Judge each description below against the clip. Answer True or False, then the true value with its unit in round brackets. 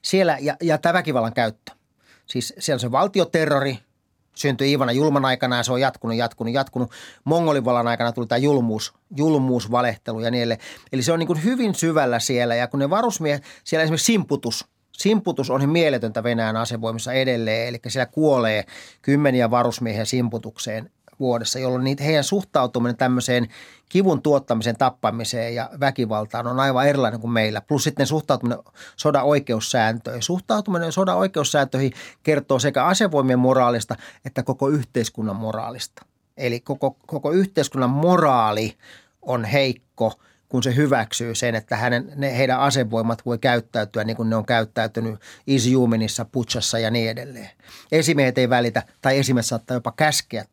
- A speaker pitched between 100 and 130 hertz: True (125 Hz)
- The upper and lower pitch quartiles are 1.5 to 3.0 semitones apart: False (3.6 semitones)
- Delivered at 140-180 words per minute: True (150 wpm)